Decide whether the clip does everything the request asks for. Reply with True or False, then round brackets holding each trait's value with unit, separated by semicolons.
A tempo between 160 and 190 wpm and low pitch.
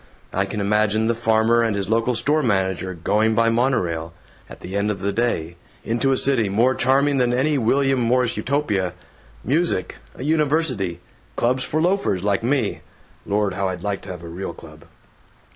True (175 wpm; 110 Hz)